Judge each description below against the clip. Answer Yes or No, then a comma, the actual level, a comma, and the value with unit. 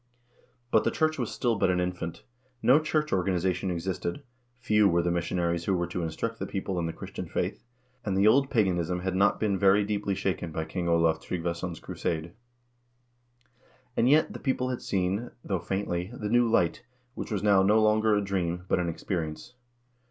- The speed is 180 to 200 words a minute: Yes, average, 185 wpm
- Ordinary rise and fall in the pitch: Yes, average, 3.7 semitones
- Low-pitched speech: Yes, very low, 95 Hz